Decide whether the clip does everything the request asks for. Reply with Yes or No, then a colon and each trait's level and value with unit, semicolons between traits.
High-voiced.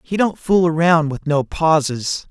No: medium, 160 Hz